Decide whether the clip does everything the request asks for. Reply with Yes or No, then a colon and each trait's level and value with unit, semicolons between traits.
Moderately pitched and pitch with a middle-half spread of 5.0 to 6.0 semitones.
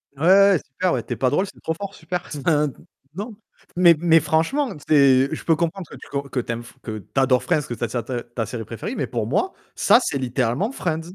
Yes: medium, 150 Hz; wide, 5.6 semitones